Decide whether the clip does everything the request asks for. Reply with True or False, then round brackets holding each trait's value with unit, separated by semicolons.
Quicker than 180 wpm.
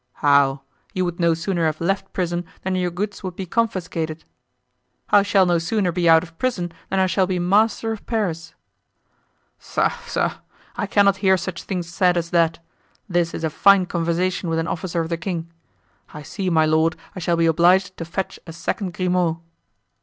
True (190 wpm)